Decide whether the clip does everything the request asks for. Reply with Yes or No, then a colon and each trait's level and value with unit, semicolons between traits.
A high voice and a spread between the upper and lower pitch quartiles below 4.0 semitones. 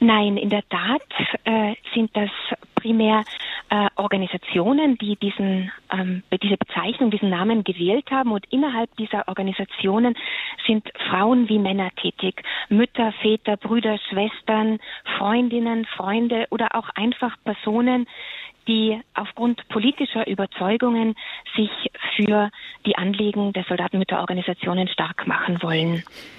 Yes: high, 215 Hz; average, 2.9 semitones